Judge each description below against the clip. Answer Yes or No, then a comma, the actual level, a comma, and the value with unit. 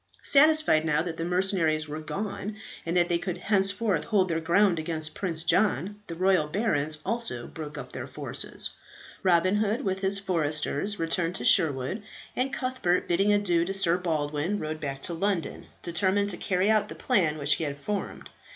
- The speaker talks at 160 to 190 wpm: Yes, average, 175 wpm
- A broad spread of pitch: No, average, 4.2 semitones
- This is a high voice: No, medium, 175 Hz